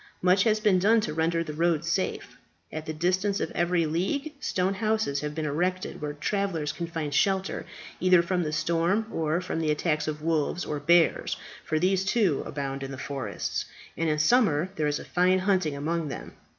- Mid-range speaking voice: Yes, medium, 170 Hz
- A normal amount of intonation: Yes, average, 3.6 semitones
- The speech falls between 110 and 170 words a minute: No, average, 190 wpm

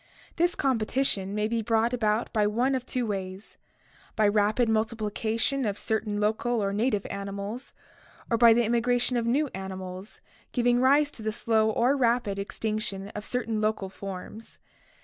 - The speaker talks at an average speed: Yes, average, 160 wpm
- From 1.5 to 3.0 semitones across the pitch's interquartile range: Yes, average, 2.7 semitones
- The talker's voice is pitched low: No, high, 220 Hz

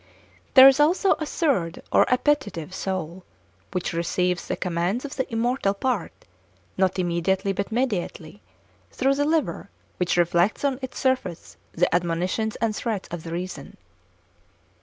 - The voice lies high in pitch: Yes, high, 195 Hz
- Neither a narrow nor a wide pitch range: No, wide, 6.9 semitones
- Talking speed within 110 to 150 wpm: Yes, average, 140 wpm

